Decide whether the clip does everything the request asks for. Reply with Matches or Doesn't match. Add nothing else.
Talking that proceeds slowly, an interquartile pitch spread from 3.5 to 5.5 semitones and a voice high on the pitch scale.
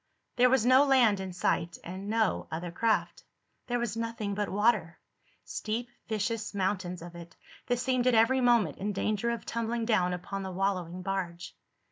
Doesn't match